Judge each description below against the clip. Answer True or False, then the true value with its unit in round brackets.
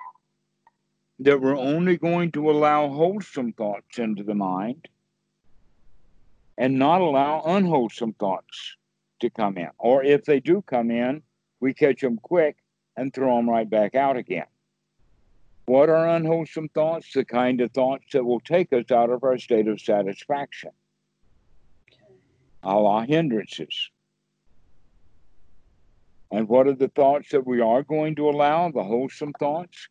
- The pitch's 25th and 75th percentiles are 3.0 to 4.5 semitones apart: False (4.9 semitones)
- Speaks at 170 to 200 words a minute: False (140 wpm)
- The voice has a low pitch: True (130 Hz)